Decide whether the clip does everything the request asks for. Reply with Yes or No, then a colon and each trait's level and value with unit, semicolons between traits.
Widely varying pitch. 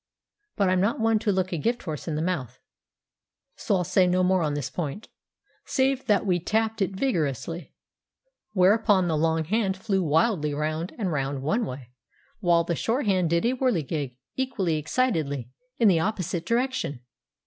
Yes: wide, 5.7 semitones